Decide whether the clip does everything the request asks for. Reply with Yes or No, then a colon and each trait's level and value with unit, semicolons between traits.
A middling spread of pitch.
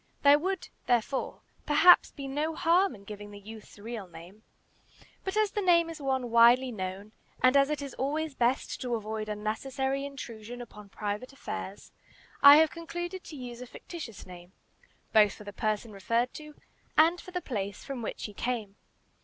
No: wide, 5.9 semitones